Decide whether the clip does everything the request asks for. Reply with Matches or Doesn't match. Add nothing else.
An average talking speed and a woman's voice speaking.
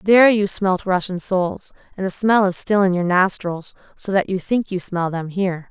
Doesn't match